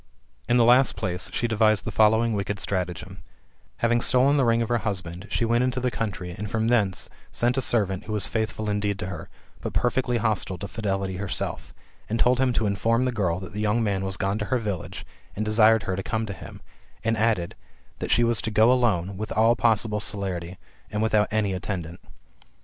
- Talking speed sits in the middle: No, fast, 210 wpm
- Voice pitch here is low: Yes, low, 110 Hz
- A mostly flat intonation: No, average, 3.2 semitones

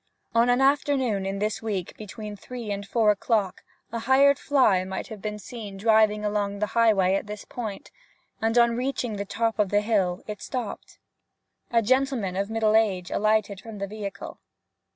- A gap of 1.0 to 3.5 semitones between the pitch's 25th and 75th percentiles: Yes, narrow, 2.5 semitones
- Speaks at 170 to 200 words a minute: Yes, average, 175 wpm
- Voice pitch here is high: Yes, high, 215 Hz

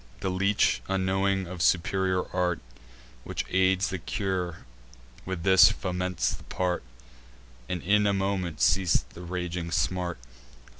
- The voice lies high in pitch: No, very low, 90 Hz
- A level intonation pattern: Yes, narrow, 1.4 semitones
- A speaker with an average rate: No, slow, 130 wpm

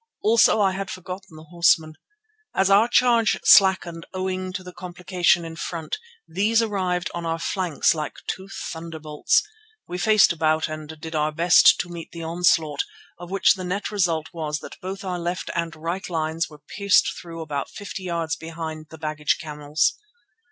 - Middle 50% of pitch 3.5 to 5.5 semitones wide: No, average, 2.9 semitones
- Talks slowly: No, average, 170 wpm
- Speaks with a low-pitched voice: No, medium, 170 Hz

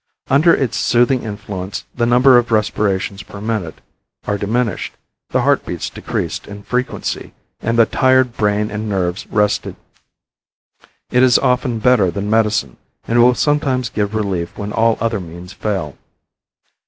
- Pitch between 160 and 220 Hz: No, low, 110 Hz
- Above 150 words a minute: No, average, 145 wpm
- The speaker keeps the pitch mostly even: No, average, 3.4 semitones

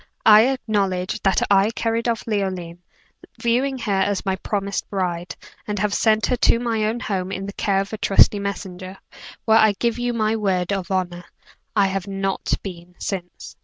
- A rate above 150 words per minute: Yes, average, 180 wpm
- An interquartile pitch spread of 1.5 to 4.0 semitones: Yes, narrow, 2.5 semitones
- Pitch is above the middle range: Yes, high, 200 Hz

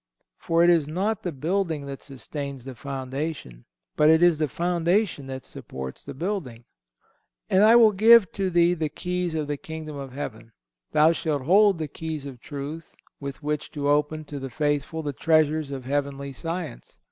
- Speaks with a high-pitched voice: No, medium, 150 Hz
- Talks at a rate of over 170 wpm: Yes, average, 180 wpm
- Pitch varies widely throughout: No, average, 3.5 semitones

